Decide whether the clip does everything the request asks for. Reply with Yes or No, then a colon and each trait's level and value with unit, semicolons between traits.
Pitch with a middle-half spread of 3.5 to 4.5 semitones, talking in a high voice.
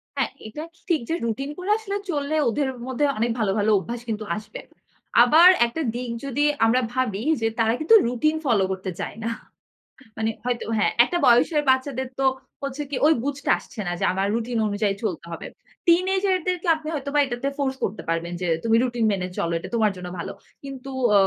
No: average, 5.1 semitones; high, 245 Hz